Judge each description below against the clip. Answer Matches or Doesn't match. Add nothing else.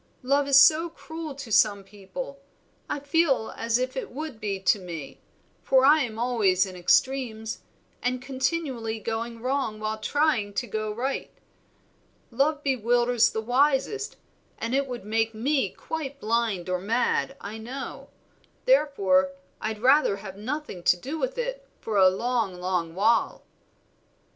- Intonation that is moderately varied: Matches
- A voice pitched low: Doesn't match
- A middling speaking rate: Matches